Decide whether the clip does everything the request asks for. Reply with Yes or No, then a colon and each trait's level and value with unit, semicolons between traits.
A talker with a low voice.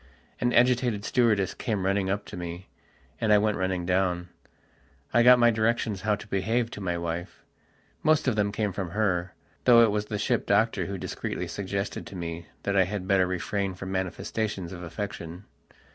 Yes: low, 100 Hz